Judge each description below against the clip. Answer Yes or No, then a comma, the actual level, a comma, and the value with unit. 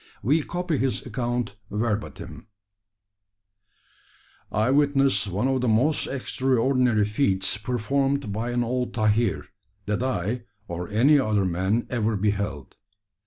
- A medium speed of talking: No, slow, 120 wpm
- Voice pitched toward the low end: Yes, low, 120 Hz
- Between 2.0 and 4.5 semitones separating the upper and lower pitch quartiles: Yes, average, 4.0 semitones